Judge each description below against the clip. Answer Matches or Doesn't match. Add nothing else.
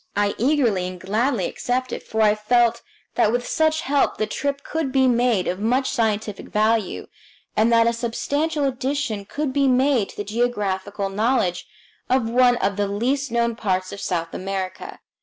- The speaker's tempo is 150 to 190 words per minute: Matches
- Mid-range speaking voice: Doesn't match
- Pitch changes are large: Doesn't match